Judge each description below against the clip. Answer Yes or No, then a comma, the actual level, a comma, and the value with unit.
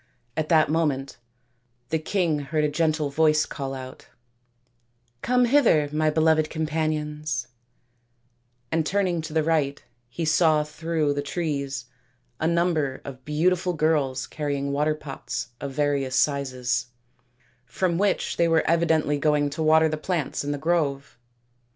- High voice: No, medium, 155 Hz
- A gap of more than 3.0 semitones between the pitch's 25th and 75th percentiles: No, narrow, 2.4 semitones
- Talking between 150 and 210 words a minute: No, average, 140 wpm